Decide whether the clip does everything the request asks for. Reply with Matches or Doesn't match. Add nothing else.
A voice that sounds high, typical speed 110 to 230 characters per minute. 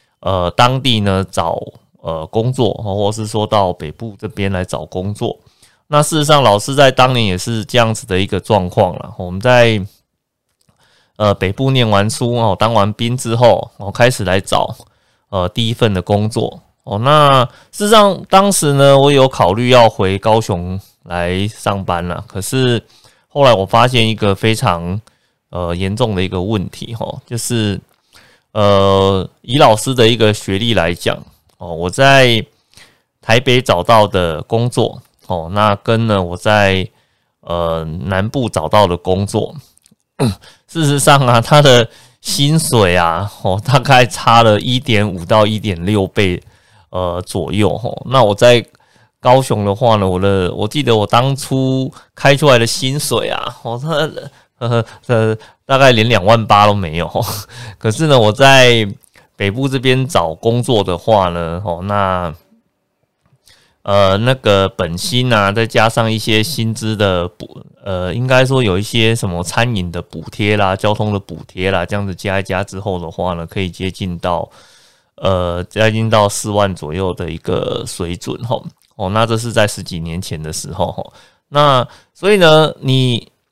Doesn't match